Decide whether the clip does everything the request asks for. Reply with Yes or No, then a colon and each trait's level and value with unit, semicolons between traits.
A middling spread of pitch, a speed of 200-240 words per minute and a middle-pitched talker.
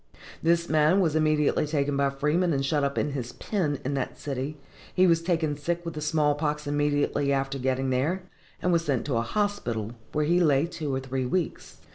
Yes: average, 3.2 semitones; fast, 205 wpm; medium, 150 Hz